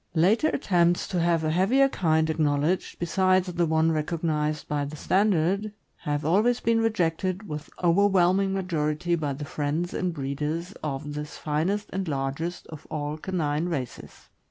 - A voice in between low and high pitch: Yes, medium, 165 Hz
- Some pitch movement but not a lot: Yes, average, 3.7 semitones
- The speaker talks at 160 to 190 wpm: No, average, 150 wpm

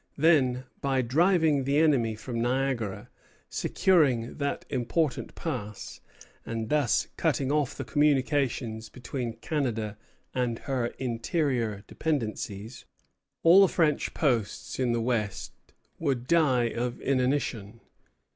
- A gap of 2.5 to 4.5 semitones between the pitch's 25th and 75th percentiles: Yes, average, 4.0 semitones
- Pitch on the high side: No, low, 130 Hz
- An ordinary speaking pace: No, slow, 110 wpm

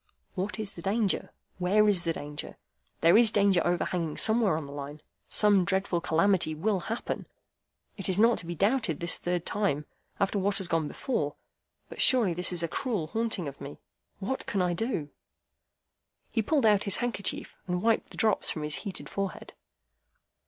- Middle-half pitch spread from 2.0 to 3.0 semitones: No, average, 4.1 semitones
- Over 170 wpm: Yes, average, 180 wpm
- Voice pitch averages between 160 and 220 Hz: Yes, high, 190 Hz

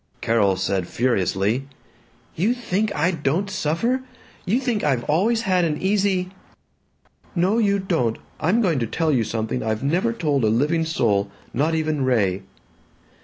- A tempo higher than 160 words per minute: No, average, 155 wpm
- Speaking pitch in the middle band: Yes, medium, 155 Hz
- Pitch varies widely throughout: Yes, wide, 8.5 semitones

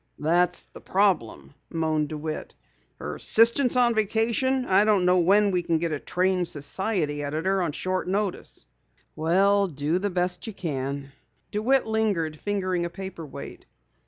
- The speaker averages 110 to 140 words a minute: No, average, 155 wpm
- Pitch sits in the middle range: Yes, medium, 180 Hz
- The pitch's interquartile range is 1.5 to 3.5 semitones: No, average, 4.3 semitones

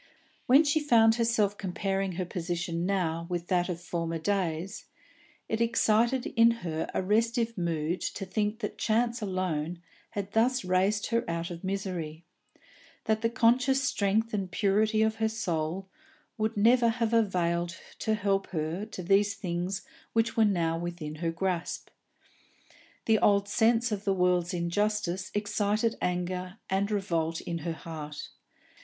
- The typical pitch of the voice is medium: No, high, 195 Hz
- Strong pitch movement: No, average, 4.1 semitones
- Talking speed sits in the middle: Yes, average, 150 wpm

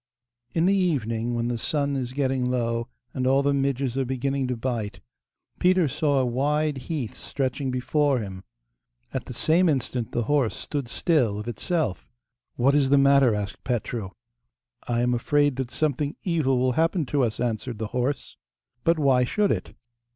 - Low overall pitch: Yes, low, 130 Hz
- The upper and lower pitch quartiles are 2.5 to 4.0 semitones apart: Yes, average, 3.3 semitones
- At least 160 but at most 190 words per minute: Yes, average, 175 wpm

